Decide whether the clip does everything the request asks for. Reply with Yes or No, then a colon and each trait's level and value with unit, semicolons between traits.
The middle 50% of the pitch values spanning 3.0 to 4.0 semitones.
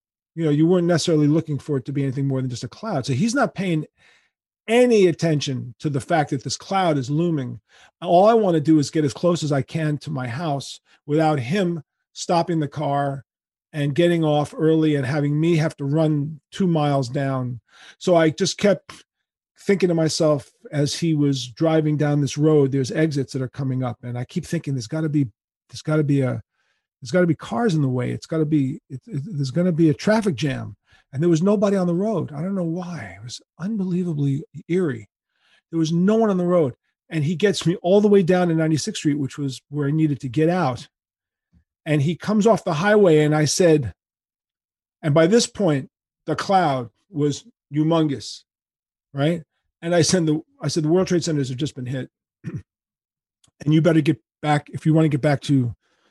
Yes: average, 3.6 semitones